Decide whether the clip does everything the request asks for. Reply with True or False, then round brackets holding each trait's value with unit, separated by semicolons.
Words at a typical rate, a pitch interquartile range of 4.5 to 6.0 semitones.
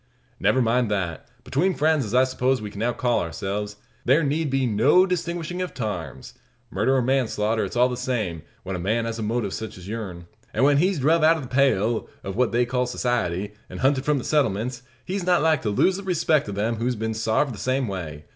False (230 wpm; 5.2 semitones)